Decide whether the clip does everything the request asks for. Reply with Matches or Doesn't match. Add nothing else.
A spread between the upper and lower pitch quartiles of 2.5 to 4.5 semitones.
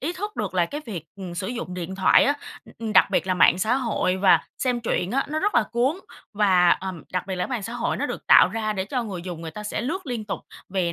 Doesn't match